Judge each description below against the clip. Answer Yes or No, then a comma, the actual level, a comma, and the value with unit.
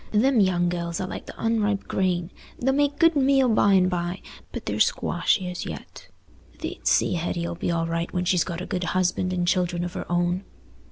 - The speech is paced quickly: Yes, fast, 210 wpm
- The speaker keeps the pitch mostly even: No, average, 3.0 semitones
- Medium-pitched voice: Yes, medium, 180 Hz